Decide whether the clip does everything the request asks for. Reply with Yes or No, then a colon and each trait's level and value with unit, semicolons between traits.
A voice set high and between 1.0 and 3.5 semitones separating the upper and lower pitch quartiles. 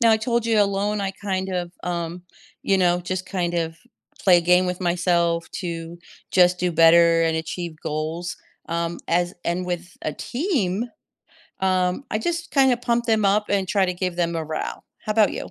No: medium, 180 Hz; average, 2.9 semitones